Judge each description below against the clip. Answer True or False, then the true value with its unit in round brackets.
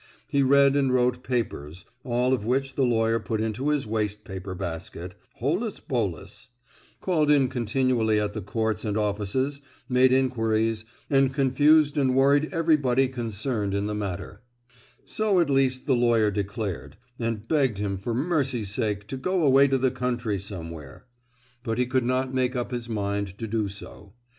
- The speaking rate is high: False (160 wpm)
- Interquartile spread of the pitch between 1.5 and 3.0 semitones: False (4.2 semitones)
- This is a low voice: True (120 Hz)